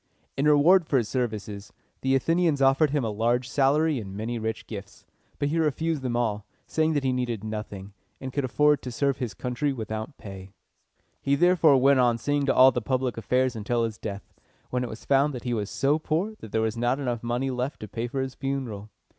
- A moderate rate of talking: No, fast, 215 wpm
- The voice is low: Yes, low, 125 Hz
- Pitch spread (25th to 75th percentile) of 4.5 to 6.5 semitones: No, average, 3.8 semitones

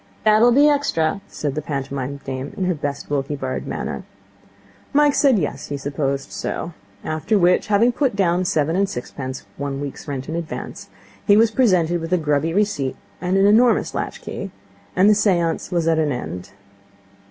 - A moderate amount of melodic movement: No, wide, 6.2 semitones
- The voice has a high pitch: No, medium, 165 Hz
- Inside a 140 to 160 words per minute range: No, average, 175 wpm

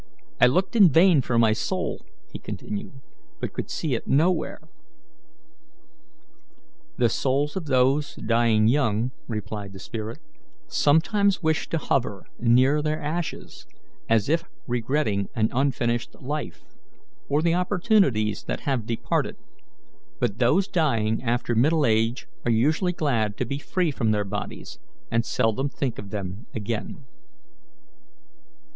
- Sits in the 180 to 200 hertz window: No, low, 125 Hz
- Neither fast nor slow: No, slow, 130 wpm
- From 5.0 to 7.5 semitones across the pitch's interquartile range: Yes, wide, 5.5 semitones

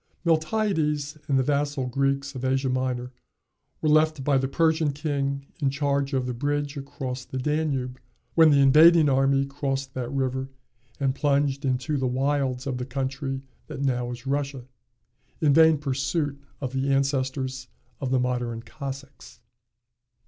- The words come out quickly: No, average, 150 wpm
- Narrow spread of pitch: Yes, narrow, 1.8 semitones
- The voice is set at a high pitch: No, low, 135 Hz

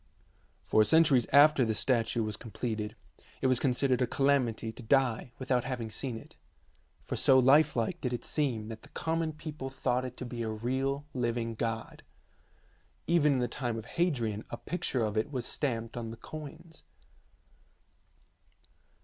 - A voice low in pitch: Yes, low, 125 Hz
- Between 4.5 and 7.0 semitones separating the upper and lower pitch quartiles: No, average, 3.4 semitones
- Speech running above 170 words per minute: No, average, 160 wpm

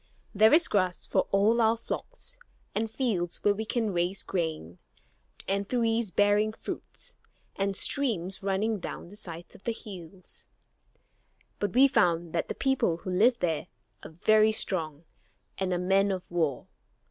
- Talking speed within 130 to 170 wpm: Yes, average, 155 wpm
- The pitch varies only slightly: No, average, 4.1 semitones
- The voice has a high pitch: Yes, high, 200 Hz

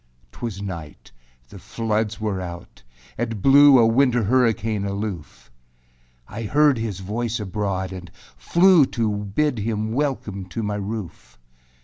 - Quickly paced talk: No, slow, 135 wpm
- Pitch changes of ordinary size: Yes, average, 3.4 semitones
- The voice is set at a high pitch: No, low, 110 Hz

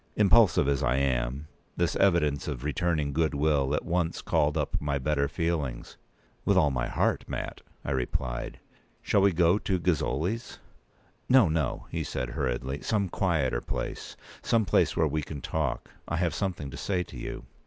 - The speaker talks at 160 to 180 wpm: Yes, average, 165 wpm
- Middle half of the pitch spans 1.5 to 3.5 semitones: No, average, 4.4 semitones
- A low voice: Yes, very low, 75 Hz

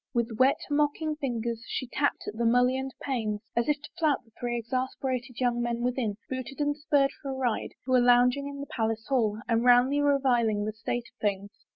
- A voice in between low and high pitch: No, high, 245 Hz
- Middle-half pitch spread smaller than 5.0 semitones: Yes, average, 2.8 semitones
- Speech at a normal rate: No, fast, 210 wpm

